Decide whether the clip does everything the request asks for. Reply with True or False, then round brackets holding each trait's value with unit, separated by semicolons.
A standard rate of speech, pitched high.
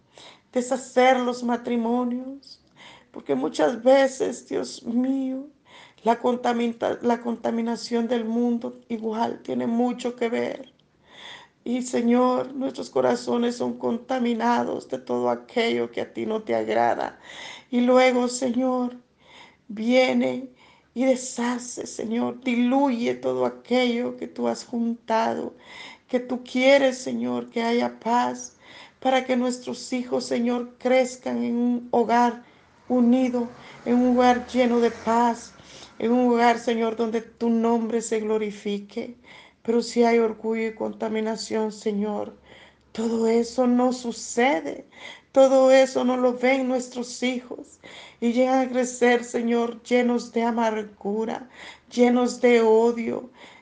False (120 wpm; 240 Hz)